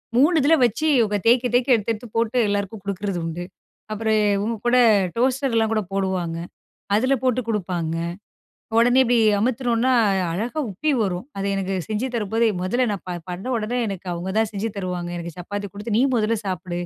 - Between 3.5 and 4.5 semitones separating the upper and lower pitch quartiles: Yes, average, 4.0 semitones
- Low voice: No, high, 215 Hz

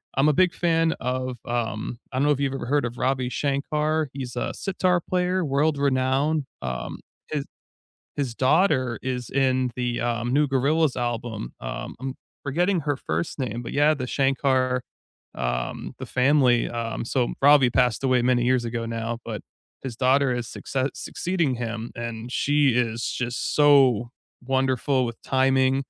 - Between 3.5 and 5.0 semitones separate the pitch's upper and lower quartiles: No, average, 2.9 semitones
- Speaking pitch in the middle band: No, low, 130 Hz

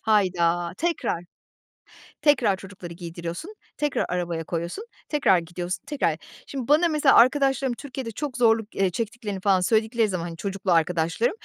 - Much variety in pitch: Yes, wide, 6.9 semitones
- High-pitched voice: Yes, high, 200 Hz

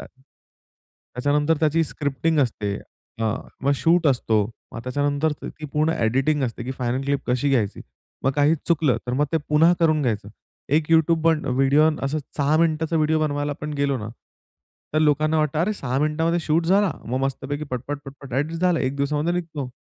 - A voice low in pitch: No, medium, 145 Hz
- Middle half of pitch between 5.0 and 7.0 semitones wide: No, average, 2.9 semitones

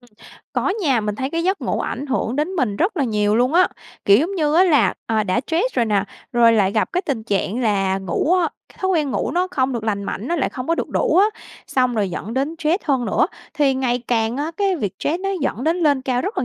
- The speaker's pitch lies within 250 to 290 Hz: Yes, very high, 260 Hz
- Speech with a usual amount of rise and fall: No, wide, 6.8 semitones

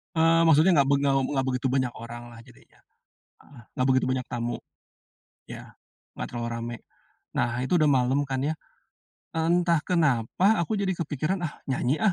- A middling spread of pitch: Yes, average, 5.0 semitones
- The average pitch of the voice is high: No, medium, 140 Hz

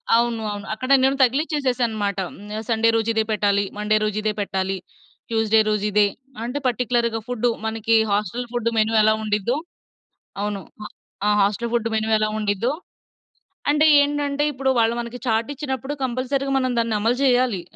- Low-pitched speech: No, high, 230 Hz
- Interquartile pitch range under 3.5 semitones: Yes, average, 3.0 semitones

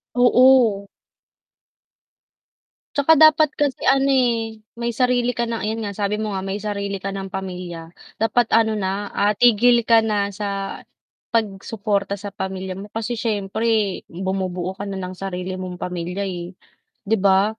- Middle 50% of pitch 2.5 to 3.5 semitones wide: Yes, average, 3.1 semitones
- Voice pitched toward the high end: Yes, high, 205 Hz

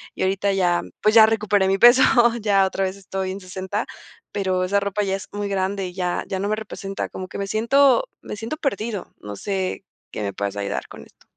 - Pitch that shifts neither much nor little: No, narrow, 2.0 semitones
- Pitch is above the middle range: Yes, high, 195 Hz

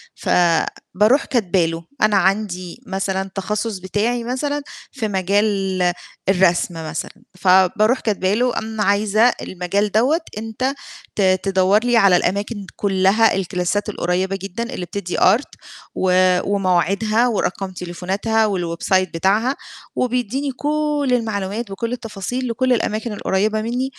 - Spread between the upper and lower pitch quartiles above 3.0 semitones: Yes, average, 3.6 semitones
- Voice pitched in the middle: No, high, 205 Hz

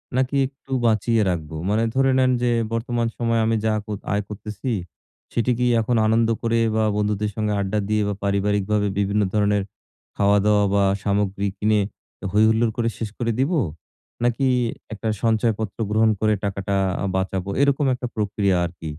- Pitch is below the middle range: Yes, low, 110 Hz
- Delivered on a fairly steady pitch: Yes, narrow, 2.3 semitones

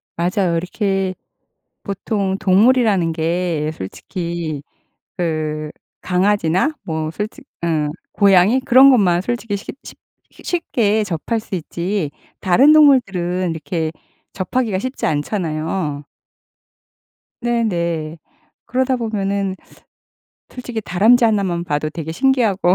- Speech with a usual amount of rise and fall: Yes, average, 5.0 semitones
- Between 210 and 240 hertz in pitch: No, medium, 185 Hz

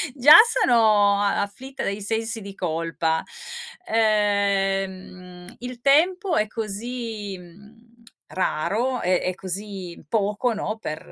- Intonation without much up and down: No, average, 3.3 semitones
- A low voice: No, high, 205 Hz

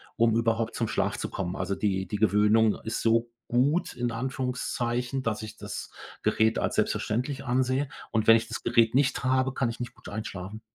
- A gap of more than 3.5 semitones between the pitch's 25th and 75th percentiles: No, narrow, 2.6 semitones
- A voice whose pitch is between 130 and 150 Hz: No, low, 115 Hz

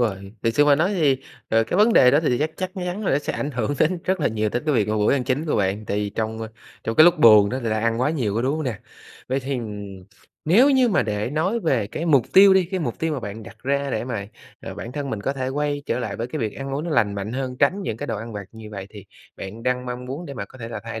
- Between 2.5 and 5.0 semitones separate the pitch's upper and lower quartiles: No, wide, 5.4 semitones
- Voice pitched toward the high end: No, low, 125 Hz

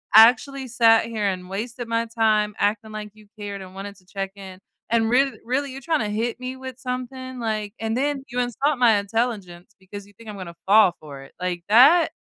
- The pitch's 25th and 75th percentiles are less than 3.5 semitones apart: No, average, 3.8 semitones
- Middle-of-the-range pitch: No, high, 220 Hz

